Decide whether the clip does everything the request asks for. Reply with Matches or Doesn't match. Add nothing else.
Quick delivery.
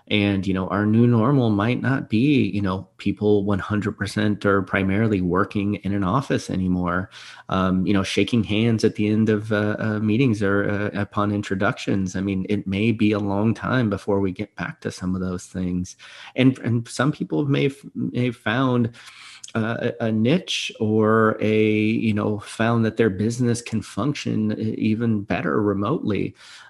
Doesn't match